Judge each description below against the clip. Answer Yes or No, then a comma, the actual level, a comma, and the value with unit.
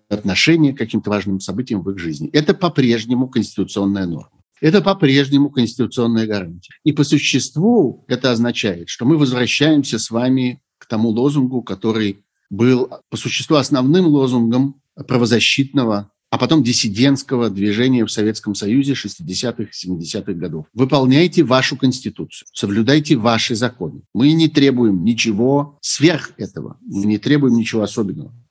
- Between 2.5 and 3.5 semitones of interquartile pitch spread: No, average, 4.6 semitones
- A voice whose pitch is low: Yes, low, 120 Hz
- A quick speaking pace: No, average, 135 wpm